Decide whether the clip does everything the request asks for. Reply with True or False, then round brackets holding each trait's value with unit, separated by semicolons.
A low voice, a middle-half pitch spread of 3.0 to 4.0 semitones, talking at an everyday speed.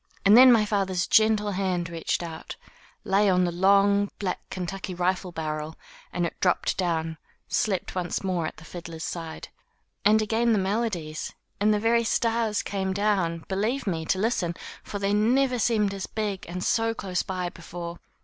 False (195 Hz; 3.4 semitones; 170 wpm)